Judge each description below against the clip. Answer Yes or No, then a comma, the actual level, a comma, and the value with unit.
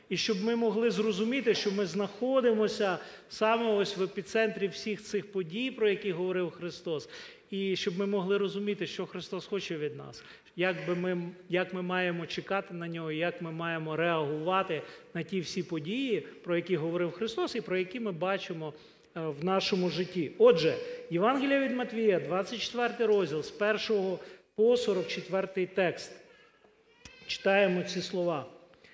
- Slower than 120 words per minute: No, average, 150 wpm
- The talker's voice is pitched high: Yes, high, 195 Hz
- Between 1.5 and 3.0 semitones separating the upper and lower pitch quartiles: No, average, 3.5 semitones